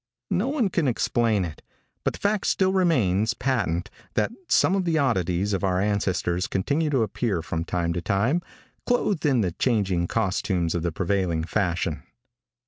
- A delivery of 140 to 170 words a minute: Yes, average, 165 wpm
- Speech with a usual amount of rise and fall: No, wide, 7.9 semitones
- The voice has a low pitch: Yes, low, 100 Hz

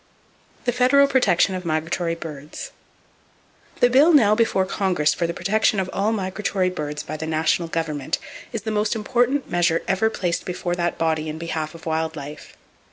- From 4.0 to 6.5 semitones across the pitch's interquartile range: Yes, average, 5.1 semitones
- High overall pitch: No, medium, 175 Hz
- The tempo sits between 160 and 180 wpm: Yes, average, 170 wpm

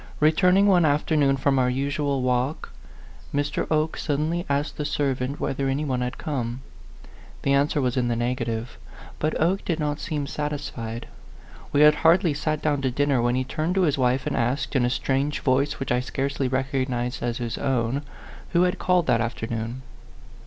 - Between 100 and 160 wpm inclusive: No, average, 180 wpm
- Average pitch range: Yes, average, 3.1 semitones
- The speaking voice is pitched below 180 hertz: Yes, medium, 140 Hz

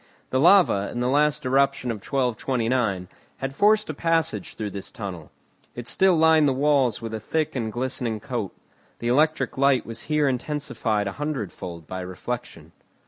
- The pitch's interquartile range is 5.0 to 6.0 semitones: Yes, wide, 5.4 semitones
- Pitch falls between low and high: No, low, 125 Hz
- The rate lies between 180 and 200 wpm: No, average, 165 wpm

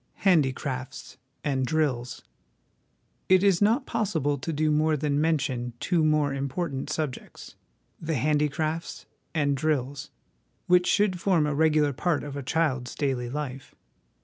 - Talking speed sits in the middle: No, slow, 130 wpm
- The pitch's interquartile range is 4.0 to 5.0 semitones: No, average, 3.0 semitones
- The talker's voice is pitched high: No, medium, 150 Hz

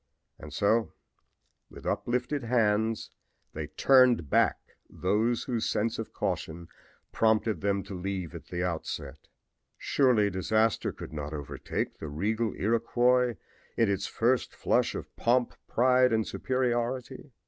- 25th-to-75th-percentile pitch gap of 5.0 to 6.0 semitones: No, average, 4.4 semitones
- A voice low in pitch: Yes, low, 110 Hz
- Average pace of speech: No, slow, 125 wpm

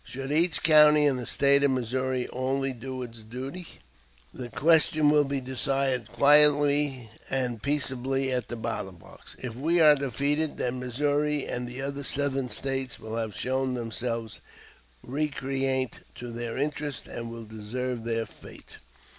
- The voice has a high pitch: No, low, 130 Hz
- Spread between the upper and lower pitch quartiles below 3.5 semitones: Yes, average, 2.8 semitones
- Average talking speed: Yes, average, 150 wpm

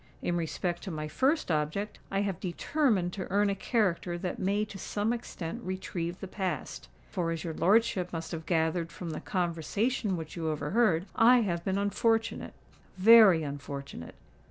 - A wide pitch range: No, average, 4.0 semitones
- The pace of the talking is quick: No, average, 155 wpm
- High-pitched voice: No, medium, 180 Hz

